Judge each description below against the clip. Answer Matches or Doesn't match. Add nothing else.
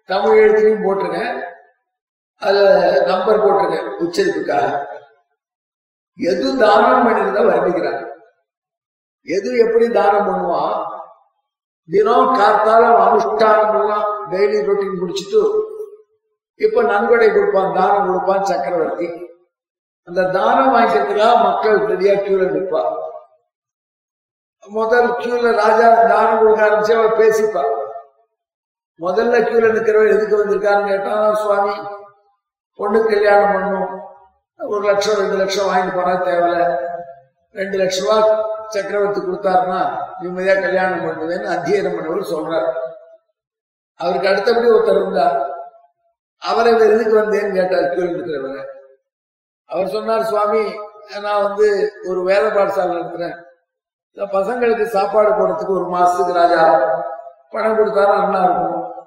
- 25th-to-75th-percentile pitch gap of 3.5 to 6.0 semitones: Doesn't match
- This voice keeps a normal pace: Matches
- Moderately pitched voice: Doesn't match